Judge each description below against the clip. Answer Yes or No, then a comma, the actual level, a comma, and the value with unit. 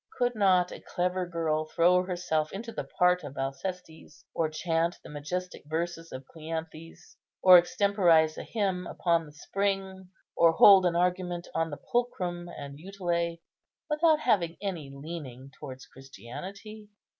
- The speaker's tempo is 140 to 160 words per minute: Yes, average, 145 wpm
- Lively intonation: No, average, 3.1 semitones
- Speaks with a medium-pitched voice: Yes, medium, 175 Hz